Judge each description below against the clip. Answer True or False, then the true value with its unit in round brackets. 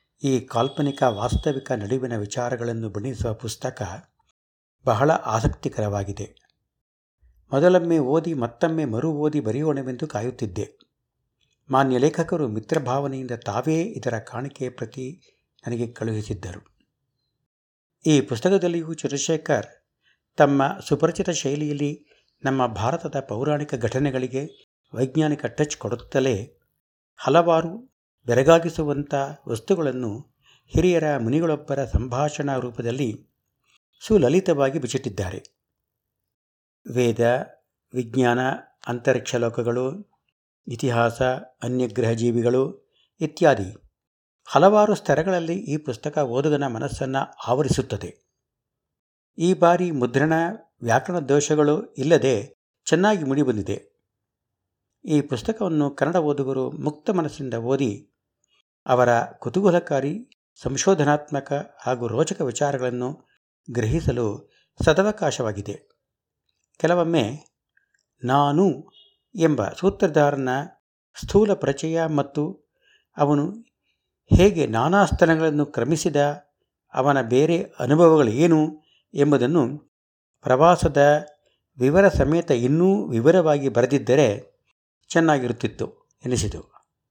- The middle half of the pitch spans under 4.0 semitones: False (4.6 semitones)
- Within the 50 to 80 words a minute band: True (75 wpm)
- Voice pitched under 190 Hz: True (140 Hz)